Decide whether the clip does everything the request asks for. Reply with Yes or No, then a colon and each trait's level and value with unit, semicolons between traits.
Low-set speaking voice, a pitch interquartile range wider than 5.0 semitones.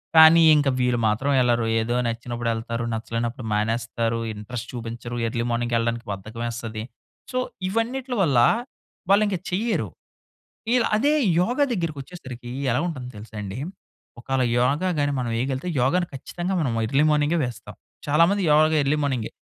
Yes: low, 125 Hz; wide, 5.5 semitones